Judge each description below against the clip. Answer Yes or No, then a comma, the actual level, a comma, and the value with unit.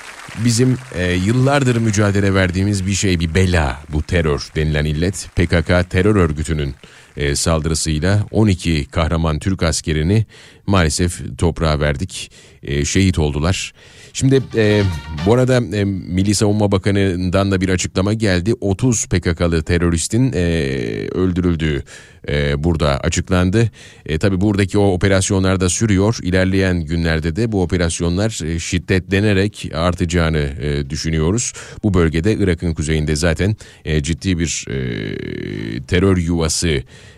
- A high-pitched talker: No, very low, 90 Hz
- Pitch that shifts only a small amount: No, average, 3.8 semitones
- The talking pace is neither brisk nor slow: Yes, average, 125 wpm